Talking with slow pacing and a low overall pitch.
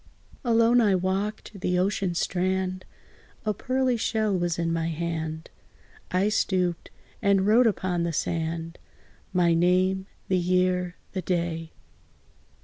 No: slow, 125 wpm; medium, 185 Hz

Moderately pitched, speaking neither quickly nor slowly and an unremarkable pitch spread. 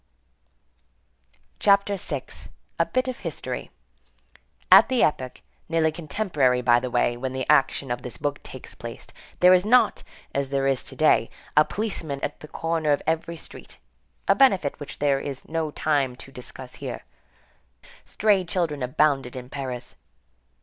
Yes: medium, 145 Hz; average, 150 wpm; average, 4.3 semitones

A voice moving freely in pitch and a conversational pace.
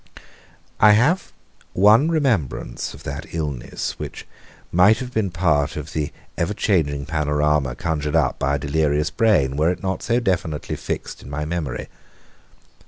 Yes: wide, 5.9 semitones; average, 150 wpm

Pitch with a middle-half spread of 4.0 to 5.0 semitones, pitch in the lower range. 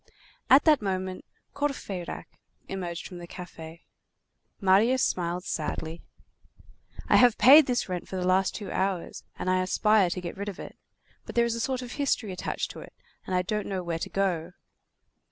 No: average, 4.3 semitones; high, 190 Hz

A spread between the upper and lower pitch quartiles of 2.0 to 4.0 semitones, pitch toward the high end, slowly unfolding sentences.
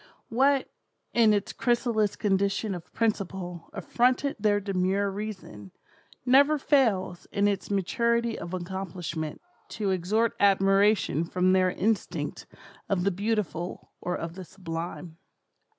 Yes: average, 3.5 semitones; high, 195 Hz; slow, 120 wpm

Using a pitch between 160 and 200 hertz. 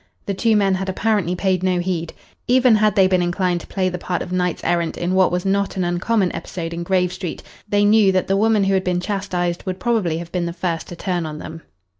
Yes: medium, 185 Hz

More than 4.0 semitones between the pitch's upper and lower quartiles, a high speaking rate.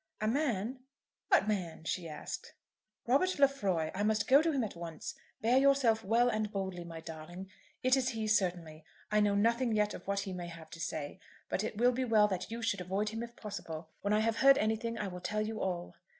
Yes: average, 4.5 semitones; fast, 220 wpm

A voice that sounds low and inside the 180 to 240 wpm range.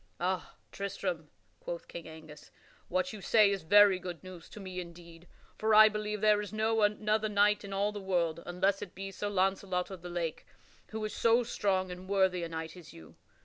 No: high, 190 Hz; average, 200 wpm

